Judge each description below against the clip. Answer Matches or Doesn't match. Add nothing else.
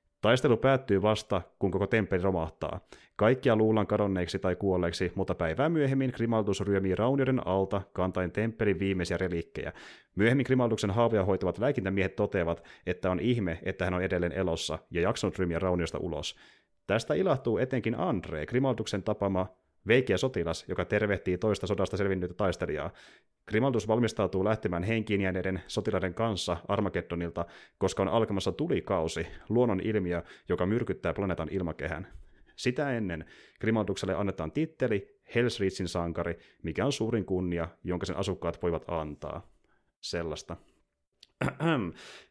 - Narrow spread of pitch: Doesn't match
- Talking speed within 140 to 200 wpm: Doesn't match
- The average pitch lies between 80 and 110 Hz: Matches